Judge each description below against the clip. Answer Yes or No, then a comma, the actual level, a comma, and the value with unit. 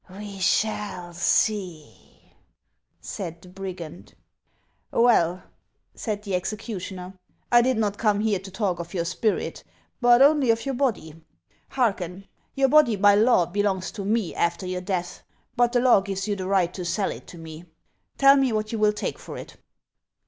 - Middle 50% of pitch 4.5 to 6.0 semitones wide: No, average, 3.8 semitones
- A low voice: No, high, 200 Hz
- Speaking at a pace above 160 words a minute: Yes, average, 180 wpm